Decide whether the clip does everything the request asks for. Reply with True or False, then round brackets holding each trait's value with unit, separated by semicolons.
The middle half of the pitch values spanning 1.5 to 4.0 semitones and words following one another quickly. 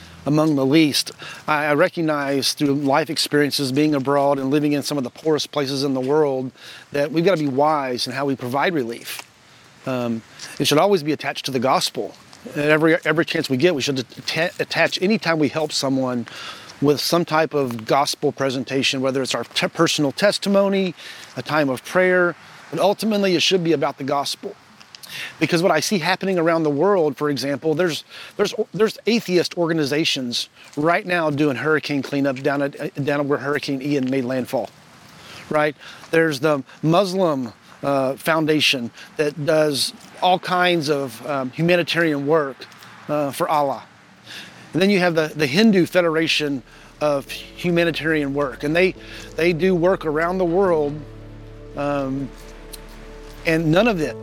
False (3.5 semitones; 165 wpm)